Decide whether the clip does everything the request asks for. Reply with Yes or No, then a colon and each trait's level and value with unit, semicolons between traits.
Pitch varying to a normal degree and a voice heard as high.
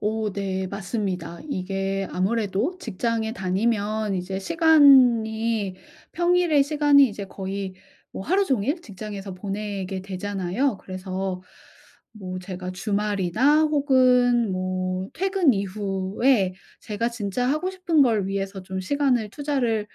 Yes: average, 5.0 semitones; high, 210 Hz